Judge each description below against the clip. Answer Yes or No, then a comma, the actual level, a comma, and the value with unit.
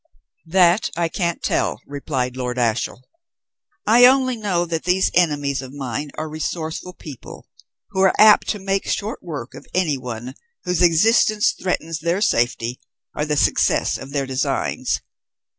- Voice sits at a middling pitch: Yes, medium, 160 Hz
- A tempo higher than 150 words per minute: No, average, 145 wpm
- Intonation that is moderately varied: No, wide, 5.8 semitones